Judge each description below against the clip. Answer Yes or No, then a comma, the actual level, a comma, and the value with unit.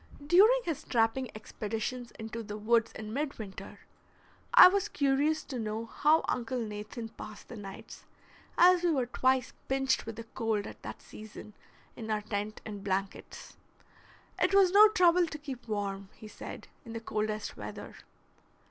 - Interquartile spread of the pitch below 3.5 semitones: No, average, 5.2 semitones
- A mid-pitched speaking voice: No, high, 230 Hz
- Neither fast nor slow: Yes, average, 155 wpm